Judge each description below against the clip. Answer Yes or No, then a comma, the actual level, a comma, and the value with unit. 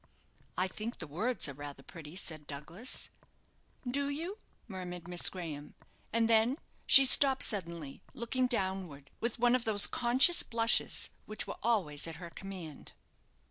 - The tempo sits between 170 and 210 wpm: No, average, 145 wpm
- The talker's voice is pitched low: No, high, 195 Hz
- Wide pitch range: Yes, wide, 6.5 semitones